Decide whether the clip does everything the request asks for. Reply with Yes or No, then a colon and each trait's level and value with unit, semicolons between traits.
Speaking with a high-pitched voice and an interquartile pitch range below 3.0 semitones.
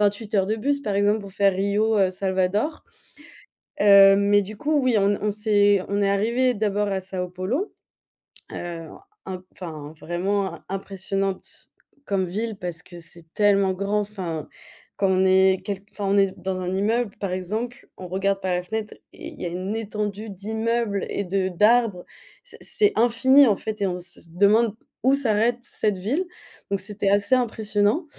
Yes: high, 200 Hz; narrow, 2.5 semitones